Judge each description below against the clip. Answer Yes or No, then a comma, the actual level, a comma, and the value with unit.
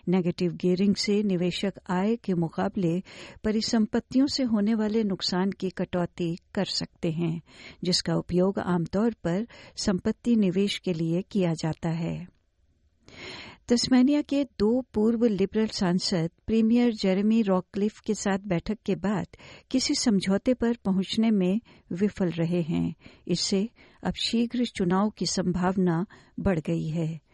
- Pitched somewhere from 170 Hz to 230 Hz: Yes, high, 190 Hz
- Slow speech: No, average, 130 wpm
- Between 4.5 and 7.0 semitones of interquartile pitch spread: No, average, 3.8 semitones